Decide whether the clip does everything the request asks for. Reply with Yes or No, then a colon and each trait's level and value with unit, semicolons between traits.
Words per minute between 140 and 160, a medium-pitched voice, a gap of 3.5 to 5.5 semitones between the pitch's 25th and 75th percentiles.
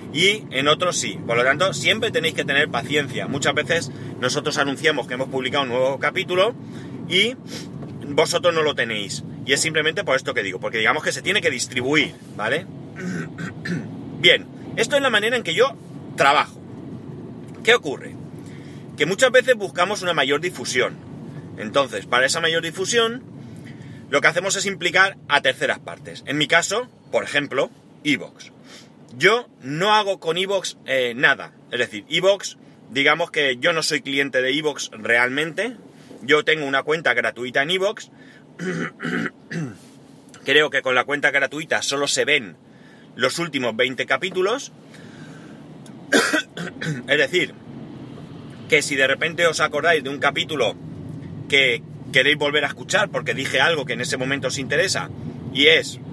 Yes: average, 155 wpm; medium, 150 Hz; average, 4.9 semitones